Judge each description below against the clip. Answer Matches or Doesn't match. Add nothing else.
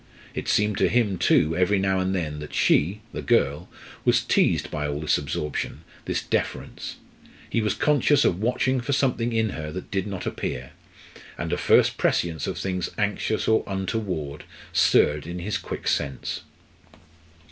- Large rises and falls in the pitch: Matches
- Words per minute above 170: Doesn't match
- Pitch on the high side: Doesn't match